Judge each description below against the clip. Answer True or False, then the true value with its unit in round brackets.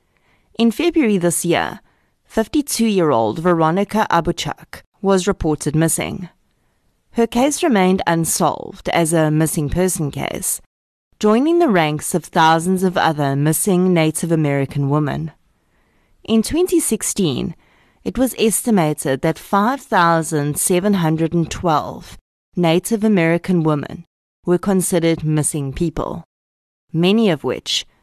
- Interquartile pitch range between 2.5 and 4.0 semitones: False (4.5 semitones)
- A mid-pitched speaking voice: True (170 Hz)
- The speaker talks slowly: True (105 wpm)